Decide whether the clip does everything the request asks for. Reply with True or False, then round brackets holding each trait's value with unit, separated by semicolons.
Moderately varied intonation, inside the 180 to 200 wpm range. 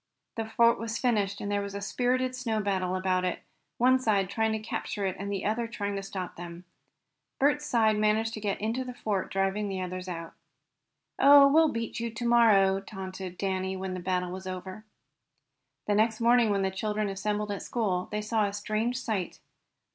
True (3.1 semitones; 195 wpm)